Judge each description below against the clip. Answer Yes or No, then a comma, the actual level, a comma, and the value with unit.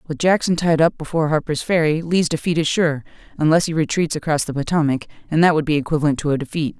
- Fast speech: Yes, fast, 220 wpm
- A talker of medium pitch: Yes, medium, 160 Hz